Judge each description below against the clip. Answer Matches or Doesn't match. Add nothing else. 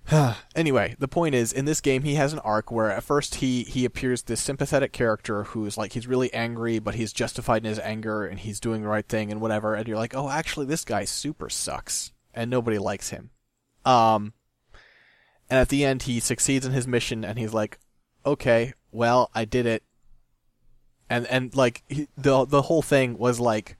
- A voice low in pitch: Matches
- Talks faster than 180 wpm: Matches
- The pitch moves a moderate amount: Matches